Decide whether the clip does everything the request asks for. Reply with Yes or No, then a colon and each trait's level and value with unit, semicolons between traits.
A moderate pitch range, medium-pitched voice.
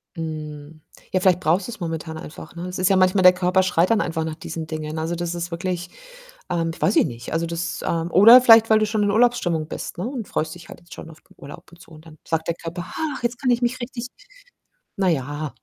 Yes: average, 3.7 semitones; medium, 175 Hz